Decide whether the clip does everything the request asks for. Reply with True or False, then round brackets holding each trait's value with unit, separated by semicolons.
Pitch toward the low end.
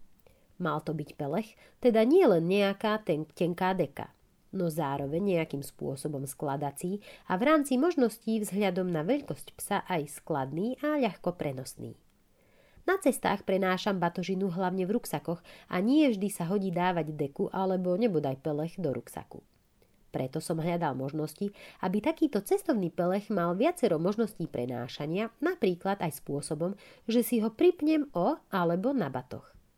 False (185 Hz)